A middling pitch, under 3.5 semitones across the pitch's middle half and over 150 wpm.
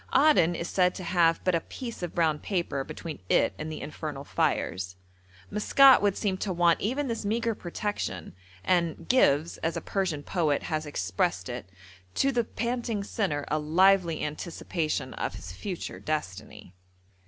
No: medium, 170 Hz; average, 5.1 semitones; average, 160 wpm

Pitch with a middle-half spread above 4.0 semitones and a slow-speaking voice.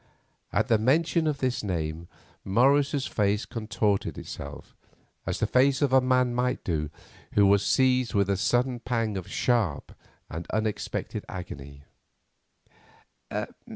Yes: average, 4.9 semitones; slow, 130 wpm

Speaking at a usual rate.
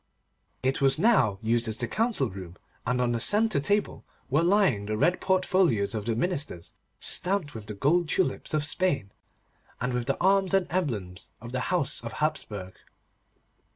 Yes: average, 170 wpm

